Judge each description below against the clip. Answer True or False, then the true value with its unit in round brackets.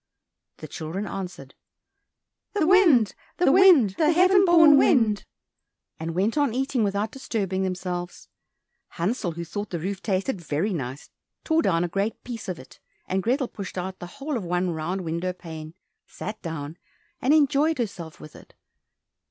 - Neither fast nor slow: True (160 wpm)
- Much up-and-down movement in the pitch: True (7.4 semitones)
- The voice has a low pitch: False (195 Hz)